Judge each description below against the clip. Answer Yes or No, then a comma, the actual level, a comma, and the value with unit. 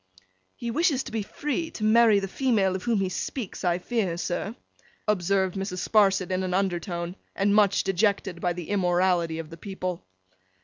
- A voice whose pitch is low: No, high, 195 Hz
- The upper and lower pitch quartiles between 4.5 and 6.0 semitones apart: No, average, 3.1 semitones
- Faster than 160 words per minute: Yes, average, 175 wpm